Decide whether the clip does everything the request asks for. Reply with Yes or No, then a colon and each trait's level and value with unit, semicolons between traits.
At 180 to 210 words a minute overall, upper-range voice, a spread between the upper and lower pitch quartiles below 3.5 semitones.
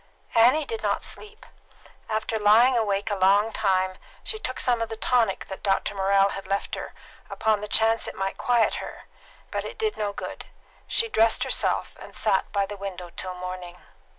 Yes: average, 190 wpm; high, 210 Hz; average, 2.9 semitones